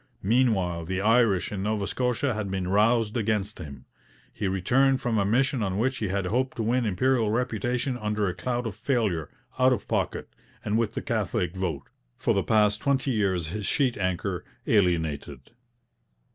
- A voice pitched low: Yes, low, 105 Hz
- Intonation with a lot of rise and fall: No, average, 4.4 semitones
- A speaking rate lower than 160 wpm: No, average, 175 wpm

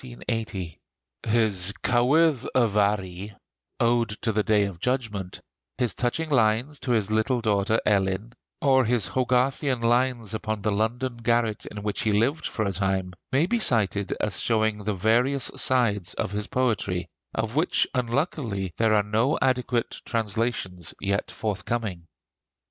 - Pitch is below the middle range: Yes, low, 110 Hz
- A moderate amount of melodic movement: Yes, average, 3.4 semitones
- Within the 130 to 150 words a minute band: Yes, average, 145 wpm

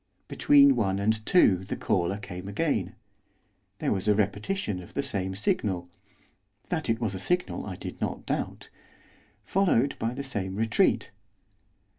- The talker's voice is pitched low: Yes, low, 105 Hz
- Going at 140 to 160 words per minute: Yes, average, 150 wpm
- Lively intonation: Yes, wide, 6.5 semitones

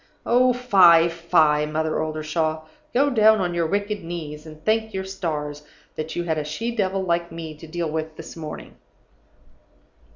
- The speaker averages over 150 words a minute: Yes, average, 170 wpm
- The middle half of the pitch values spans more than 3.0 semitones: Yes, average, 3.8 semitones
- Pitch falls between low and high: Yes, medium, 170 Hz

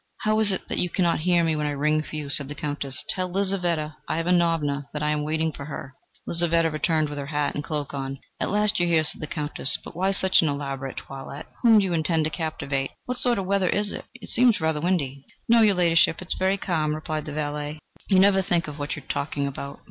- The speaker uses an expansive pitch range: No, average, 3.9 semitones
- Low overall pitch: No, medium, 160 Hz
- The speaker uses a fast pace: Yes, fast, 245 wpm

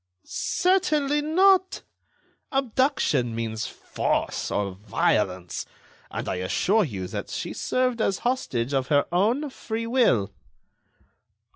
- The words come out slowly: Yes, slow, 110 wpm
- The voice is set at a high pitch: Yes, high, 215 Hz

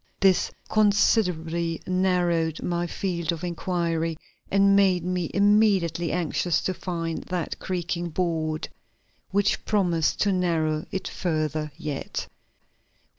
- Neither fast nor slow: No, slow, 110 wpm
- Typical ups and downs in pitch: No, narrow, 2.3 semitones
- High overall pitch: No, medium, 175 Hz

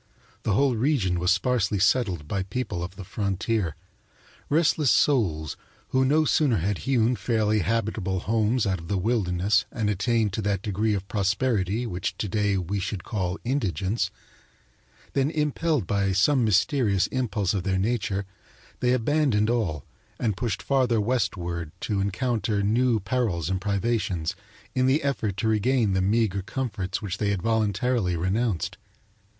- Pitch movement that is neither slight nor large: Yes, average, 4.3 semitones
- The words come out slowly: No, average, 150 wpm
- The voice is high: No, low, 105 Hz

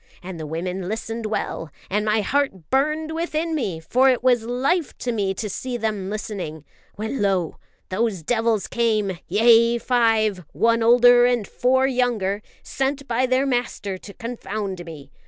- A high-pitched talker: Yes, high, 225 Hz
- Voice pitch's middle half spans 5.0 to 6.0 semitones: No, average, 4.2 semitones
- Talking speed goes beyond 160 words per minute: No, average, 155 wpm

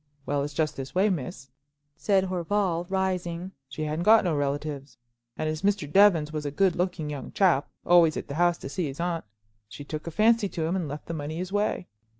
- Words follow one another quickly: Yes, fast, 215 wpm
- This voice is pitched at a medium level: Yes, medium, 170 Hz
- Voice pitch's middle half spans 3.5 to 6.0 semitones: Yes, average, 4.1 semitones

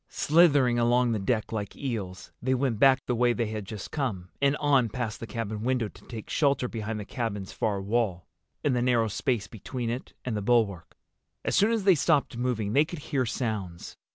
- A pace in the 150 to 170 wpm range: No, fast, 205 wpm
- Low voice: Yes, low, 120 Hz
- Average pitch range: Yes, average, 3.5 semitones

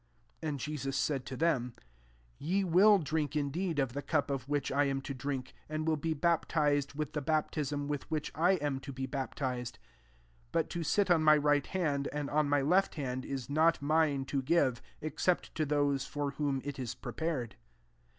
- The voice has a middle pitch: Yes, medium, 145 Hz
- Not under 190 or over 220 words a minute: Yes, average, 200 wpm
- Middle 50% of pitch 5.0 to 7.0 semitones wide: No, narrow, 2.5 semitones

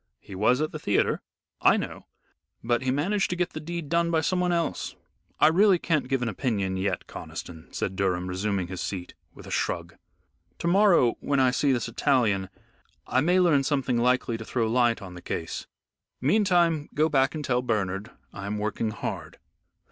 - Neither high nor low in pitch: No, low, 125 Hz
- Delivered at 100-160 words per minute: No, average, 185 wpm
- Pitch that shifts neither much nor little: No, wide, 7.8 semitones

